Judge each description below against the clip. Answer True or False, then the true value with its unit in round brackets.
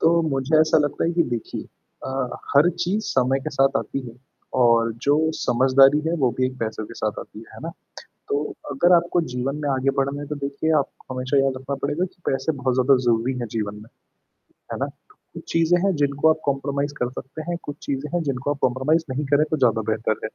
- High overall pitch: False (140 Hz)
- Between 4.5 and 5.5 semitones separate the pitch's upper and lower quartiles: False (2.7 semitones)